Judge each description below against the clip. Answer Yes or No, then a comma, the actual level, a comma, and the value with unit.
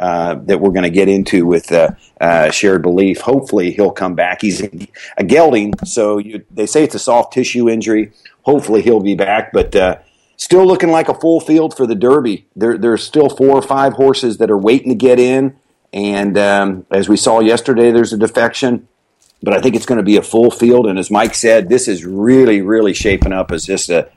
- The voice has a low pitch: Yes, low, 115 Hz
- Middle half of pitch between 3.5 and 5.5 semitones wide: Yes, average, 4.7 semitones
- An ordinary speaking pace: No, fast, 220 wpm